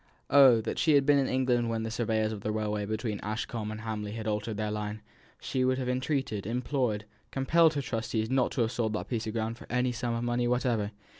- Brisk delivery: Yes, fast, 230 wpm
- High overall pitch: No, low, 115 Hz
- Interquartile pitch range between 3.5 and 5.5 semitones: No, average, 2.8 semitones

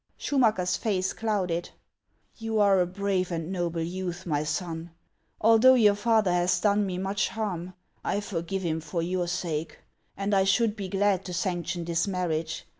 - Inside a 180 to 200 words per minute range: No, average, 170 wpm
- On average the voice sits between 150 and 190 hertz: Yes, medium, 185 Hz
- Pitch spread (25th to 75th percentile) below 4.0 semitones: Yes, average, 2.9 semitones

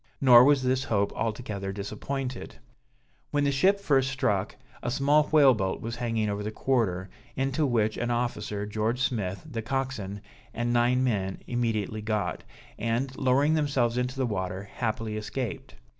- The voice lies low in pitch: Yes, low, 120 Hz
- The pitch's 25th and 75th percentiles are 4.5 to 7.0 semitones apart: No, average, 3.9 semitones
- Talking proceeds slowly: No, average, 155 wpm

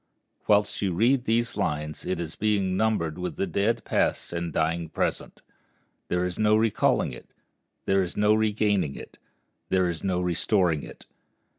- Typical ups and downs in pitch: Yes, average, 3.7 semitones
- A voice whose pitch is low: Yes, very low, 95 Hz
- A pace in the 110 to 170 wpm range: Yes, average, 160 wpm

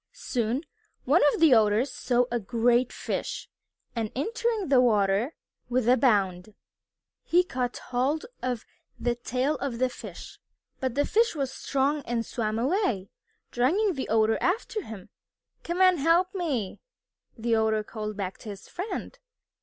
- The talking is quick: No, average, 150 wpm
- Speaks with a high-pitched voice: Yes, very high, 250 Hz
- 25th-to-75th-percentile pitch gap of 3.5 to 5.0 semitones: No, wide, 5.5 semitones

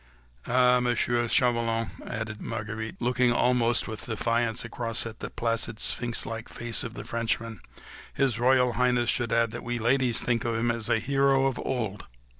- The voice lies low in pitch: Yes, low, 120 Hz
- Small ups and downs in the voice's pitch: Yes, narrow, 1.5 semitones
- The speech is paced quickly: No, average, 175 wpm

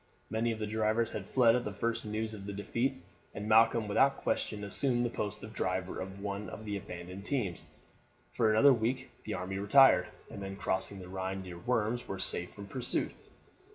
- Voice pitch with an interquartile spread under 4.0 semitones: Yes, average, 3.1 semitones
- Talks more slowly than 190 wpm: No, average, 195 wpm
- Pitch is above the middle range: No, low, 105 Hz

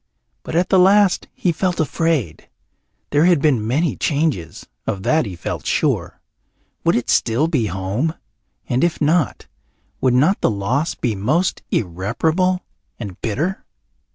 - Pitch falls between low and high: Yes, medium, 145 Hz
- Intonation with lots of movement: Yes, wide, 7.5 semitones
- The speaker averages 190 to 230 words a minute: No, average, 145 wpm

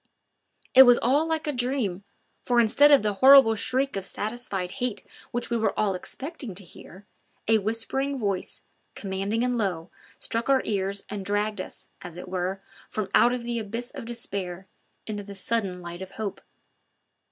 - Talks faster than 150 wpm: Yes, average, 170 wpm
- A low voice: No, high, 215 Hz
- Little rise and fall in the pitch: No, average, 4.0 semitones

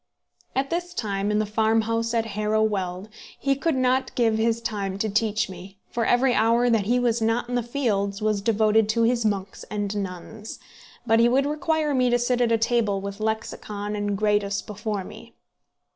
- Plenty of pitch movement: No, average, 2.7 semitones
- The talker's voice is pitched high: Yes, high, 220 Hz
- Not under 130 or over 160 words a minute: No, average, 190 wpm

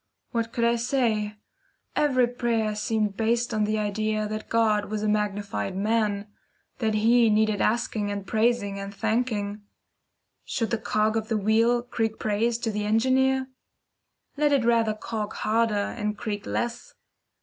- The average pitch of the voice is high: Yes, high, 220 Hz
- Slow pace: No, average, 150 wpm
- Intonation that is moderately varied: No, narrow, 1.9 semitones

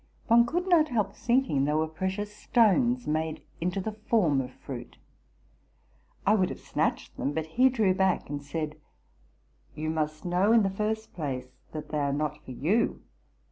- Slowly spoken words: No, average, 180 wpm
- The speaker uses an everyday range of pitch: No, wide, 6.5 semitones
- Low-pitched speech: No, medium, 180 Hz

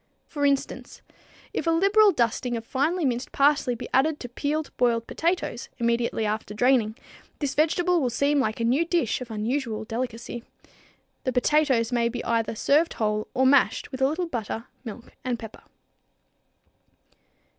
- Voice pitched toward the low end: No, very high, 250 Hz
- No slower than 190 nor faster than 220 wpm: No, average, 155 wpm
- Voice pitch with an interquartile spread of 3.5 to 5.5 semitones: Yes, average, 4.2 semitones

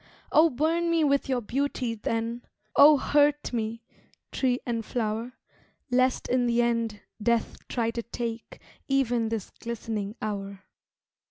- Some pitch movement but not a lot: Yes, average, 3.0 semitones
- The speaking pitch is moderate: No, high, 235 Hz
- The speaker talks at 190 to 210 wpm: No, slow, 135 wpm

